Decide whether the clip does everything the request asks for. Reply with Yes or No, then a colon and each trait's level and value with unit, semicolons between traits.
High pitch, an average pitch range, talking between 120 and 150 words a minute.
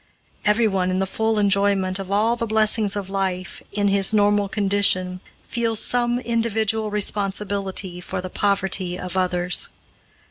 No: high, 200 Hz; narrow, 2.3 semitones; average, 140 wpm